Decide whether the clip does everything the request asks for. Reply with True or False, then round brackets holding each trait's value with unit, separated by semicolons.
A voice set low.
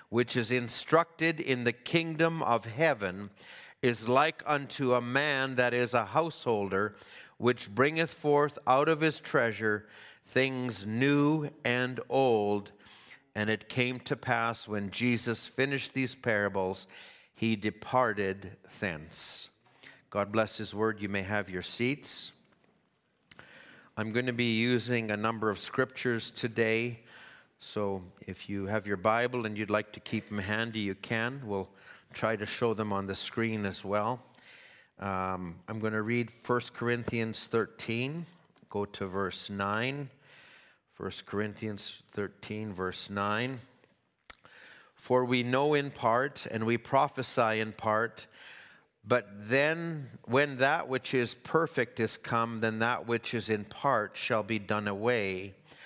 True (115 Hz)